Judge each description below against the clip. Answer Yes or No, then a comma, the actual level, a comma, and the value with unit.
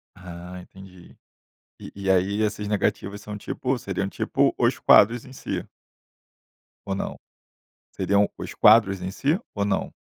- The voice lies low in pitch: Yes, low, 100 Hz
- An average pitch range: No, narrow, 1.9 semitones